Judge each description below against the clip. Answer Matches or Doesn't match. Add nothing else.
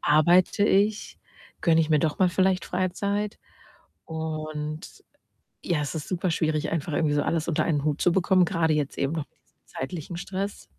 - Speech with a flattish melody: Doesn't match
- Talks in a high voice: Doesn't match